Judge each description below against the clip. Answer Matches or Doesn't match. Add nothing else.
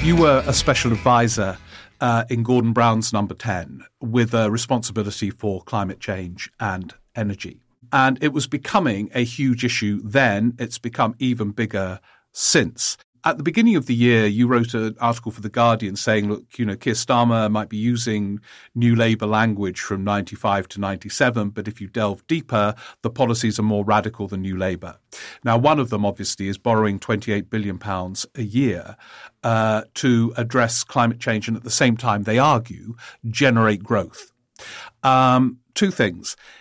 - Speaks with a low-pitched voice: Matches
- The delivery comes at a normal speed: Matches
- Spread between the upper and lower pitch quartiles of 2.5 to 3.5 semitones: Matches